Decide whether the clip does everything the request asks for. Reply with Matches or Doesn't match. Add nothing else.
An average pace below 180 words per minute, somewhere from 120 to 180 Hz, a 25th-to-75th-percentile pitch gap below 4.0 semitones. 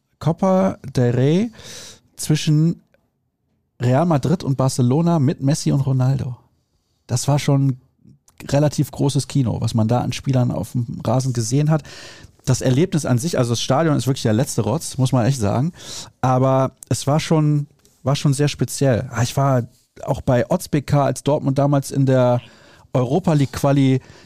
Matches